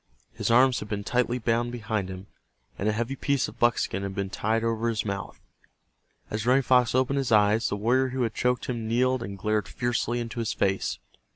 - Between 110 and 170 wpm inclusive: No, fast, 205 wpm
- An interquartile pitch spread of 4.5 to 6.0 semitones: No, average, 2.8 semitones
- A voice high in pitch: No, low, 115 Hz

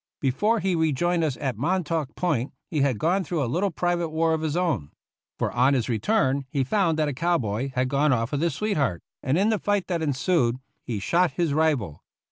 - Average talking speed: No, fast, 215 wpm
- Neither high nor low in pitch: Yes, medium, 155 Hz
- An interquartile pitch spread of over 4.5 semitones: Yes, average, 5.0 semitones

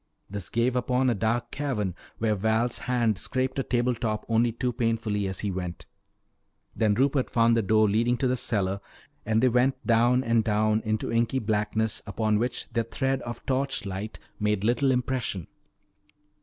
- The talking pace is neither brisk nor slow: Yes, average, 170 wpm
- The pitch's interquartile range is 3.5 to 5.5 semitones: No, average, 2.7 semitones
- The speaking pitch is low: Yes, low, 115 Hz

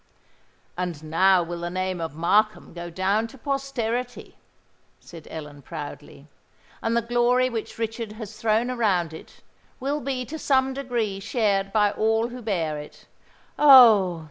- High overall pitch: Yes, high, 215 Hz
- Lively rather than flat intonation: Yes, wide, 5.8 semitones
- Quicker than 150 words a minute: No, average, 145 wpm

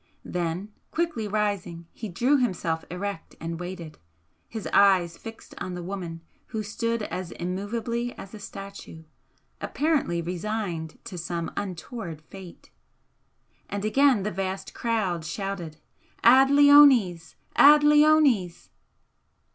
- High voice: Yes, high, 195 Hz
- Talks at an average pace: No, slow, 115 wpm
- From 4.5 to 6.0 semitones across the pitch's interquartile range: Yes, average, 5.0 semitones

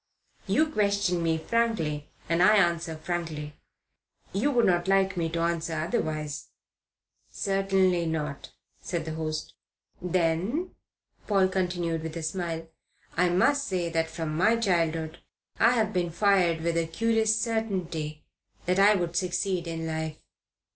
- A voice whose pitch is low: No, medium, 175 Hz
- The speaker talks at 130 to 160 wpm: Yes, average, 140 wpm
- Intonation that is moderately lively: Yes, average, 3.3 semitones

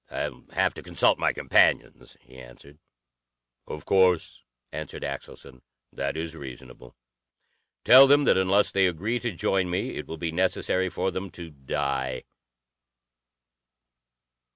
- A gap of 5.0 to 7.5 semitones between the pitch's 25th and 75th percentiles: Yes, wide, 5.4 semitones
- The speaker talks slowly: Yes, slow, 130 wpm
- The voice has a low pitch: Yes, very low, 85 Hz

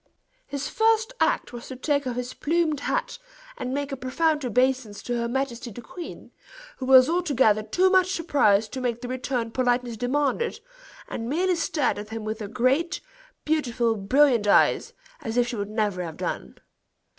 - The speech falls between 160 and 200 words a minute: Yes, average, 175 wpm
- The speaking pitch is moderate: No, very high, 255 Hz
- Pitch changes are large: No, average, 4.4 semitones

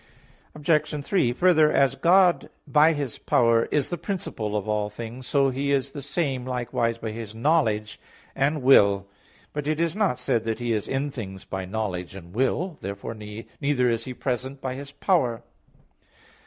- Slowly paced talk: No, average, 170 wpm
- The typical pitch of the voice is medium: No, low, 130 Hz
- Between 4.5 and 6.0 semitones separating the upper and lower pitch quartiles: Yes, average, 4.9 semitones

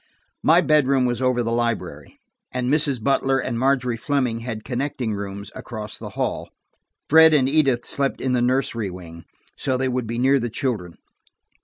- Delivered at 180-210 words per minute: No, average, 170 wpm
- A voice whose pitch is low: Yes, low, 125 Hz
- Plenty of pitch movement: No, average, 2.8 semitones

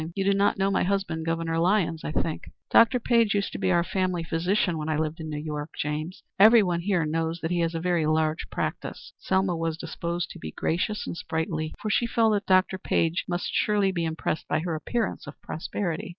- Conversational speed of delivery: No, fast, 215 wpm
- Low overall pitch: No, medium, 170 Hz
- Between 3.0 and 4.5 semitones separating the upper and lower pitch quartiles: Yes, average, 3.4 semitones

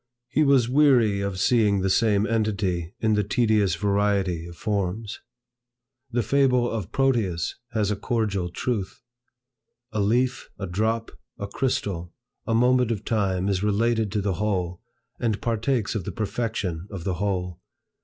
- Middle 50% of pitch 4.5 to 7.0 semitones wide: No, average, 3.2 semitones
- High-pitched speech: No, low, 105 Hz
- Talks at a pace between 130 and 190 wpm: Yes, average, 150 wpm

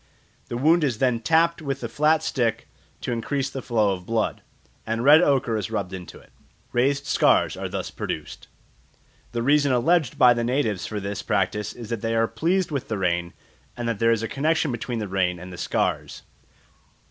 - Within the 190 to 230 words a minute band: Yes, average, 195 wpm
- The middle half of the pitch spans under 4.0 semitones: No, average, 4.6 semitones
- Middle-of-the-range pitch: No, low, 120 Hz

